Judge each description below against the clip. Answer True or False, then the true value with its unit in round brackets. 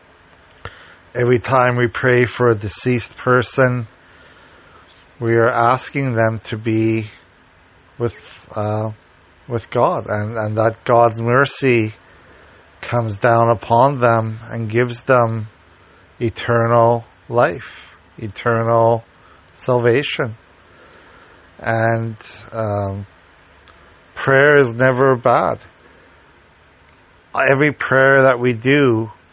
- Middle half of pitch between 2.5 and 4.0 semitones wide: True (3.1 semitones)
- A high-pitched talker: False (115 Hz)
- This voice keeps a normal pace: False (90 wpm)